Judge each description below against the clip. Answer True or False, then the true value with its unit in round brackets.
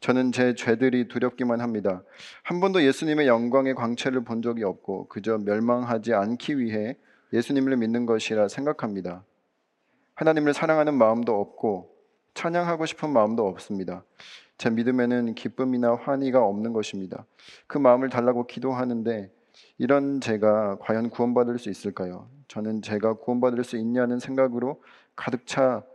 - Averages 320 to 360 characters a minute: True (335 characters per minute)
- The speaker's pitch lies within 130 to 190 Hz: False (120 Hz)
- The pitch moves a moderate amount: True (3.0 semitones)